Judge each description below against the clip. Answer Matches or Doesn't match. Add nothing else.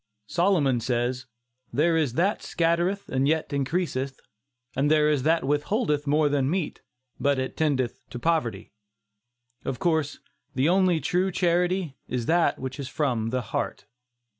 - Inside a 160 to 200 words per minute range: Doesn't match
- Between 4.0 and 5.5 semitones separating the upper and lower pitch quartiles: Matches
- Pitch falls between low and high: Matches